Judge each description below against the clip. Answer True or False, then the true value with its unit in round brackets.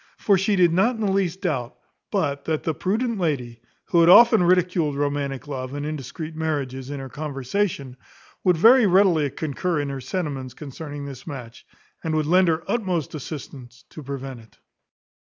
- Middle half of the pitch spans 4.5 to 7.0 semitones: True (4.9 semitones)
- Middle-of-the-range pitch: True (155 Hz)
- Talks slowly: False (175 wpm)